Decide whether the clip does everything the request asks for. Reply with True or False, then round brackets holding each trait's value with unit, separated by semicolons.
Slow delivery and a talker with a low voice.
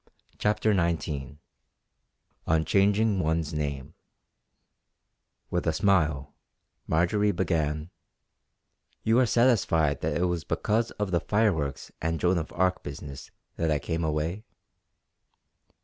True (115 wpm; 85 Hz)